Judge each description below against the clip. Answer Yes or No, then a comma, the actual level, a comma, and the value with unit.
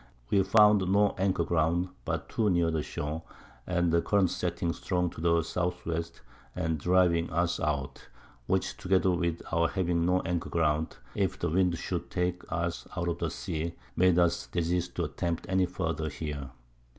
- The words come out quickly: No, average, 175 wpm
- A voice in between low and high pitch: No, very low, 85 Hz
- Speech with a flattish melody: Yes, narrow, 1.7 semitones